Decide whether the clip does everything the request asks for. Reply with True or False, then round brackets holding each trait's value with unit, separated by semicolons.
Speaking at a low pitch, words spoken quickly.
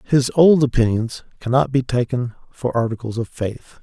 False (125 Hz; 155 wpm)